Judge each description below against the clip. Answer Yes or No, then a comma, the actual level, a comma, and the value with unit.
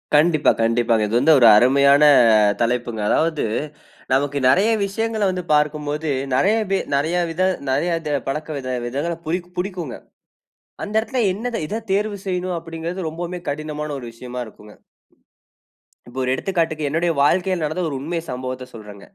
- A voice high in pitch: No, medium, 155 Hz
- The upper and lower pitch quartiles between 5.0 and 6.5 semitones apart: Yes, average, 5.3 semitones